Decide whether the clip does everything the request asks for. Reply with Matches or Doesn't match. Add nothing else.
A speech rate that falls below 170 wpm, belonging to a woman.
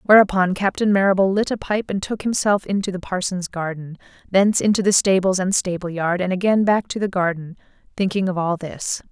Doesn't match